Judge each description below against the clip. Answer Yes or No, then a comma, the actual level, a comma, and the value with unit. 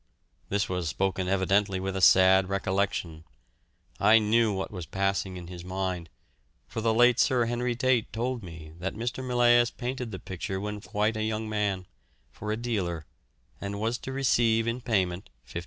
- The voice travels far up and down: No, average, 3.8 semitones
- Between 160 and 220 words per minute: Yes, average, 170 wpm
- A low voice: Yes, low, 105 Hz